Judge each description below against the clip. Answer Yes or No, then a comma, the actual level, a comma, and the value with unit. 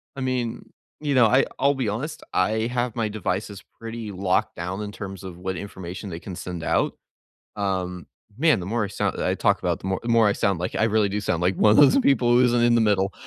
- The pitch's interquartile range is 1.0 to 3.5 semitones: No, average, 4.0 semitones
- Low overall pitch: Yes, low, 105 Hz